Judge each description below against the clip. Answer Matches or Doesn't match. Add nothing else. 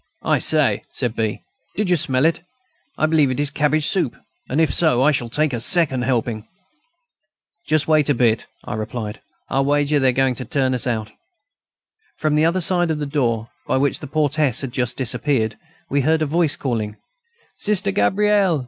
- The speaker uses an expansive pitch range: Doesn't match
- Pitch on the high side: Doesn't match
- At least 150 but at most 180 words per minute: Doesn't match